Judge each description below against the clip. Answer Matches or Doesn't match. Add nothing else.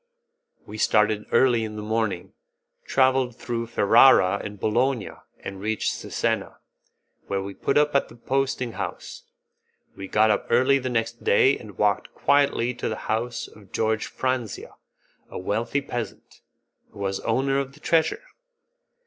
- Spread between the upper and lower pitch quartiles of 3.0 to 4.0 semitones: Matches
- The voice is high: Doesn't match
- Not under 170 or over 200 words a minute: Doesn't match